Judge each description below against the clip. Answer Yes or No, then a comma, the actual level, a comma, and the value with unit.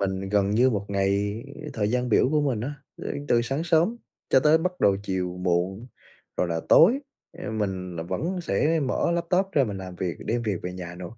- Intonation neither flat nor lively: No, wide, 7.6 semitones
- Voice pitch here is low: Yes, low, 105 Hz